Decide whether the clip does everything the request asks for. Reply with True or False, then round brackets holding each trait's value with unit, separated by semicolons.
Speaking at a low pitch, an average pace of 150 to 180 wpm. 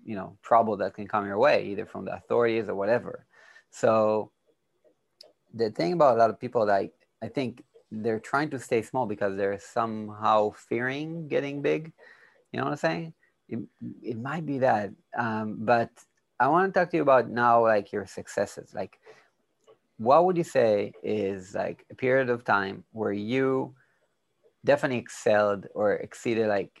True (115 Hz; 170 wpm)